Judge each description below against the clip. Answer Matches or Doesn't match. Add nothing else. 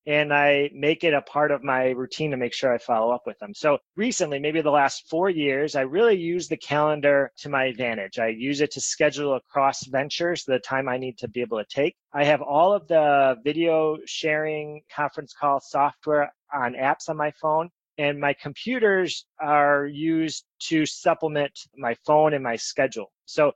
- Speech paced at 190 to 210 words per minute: Matches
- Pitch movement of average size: Doesn't match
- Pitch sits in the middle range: Matches